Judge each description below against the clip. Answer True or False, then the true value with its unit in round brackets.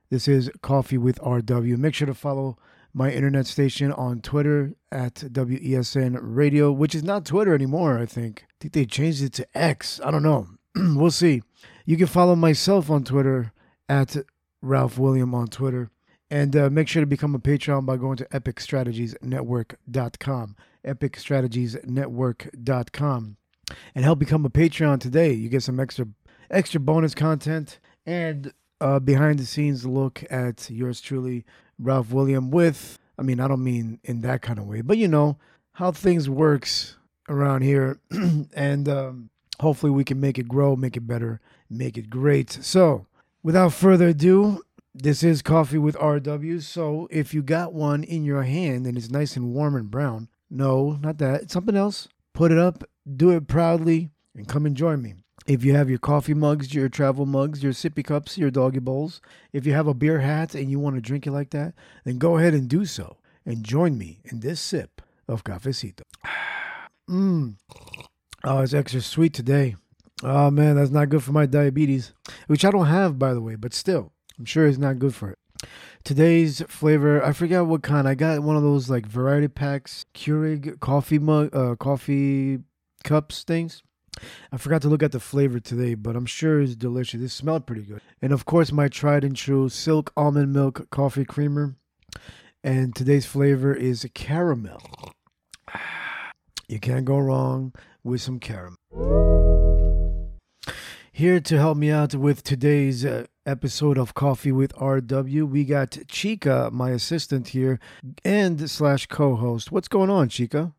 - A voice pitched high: False (140 Hz)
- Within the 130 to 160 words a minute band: False (170 wpm)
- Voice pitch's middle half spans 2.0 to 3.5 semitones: True (3.1 semitones)